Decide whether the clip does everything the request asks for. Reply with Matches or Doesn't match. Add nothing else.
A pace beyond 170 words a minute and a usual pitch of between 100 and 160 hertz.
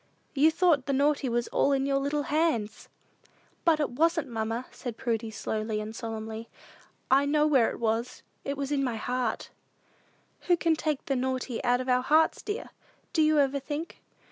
Doesn't match